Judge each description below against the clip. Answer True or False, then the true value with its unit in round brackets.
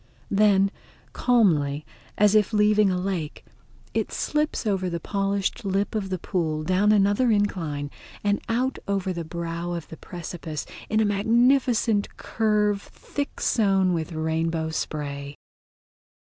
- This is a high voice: True (195 Hz)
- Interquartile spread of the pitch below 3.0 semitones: False (4.1 semitones)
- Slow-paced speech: True (130 wpm)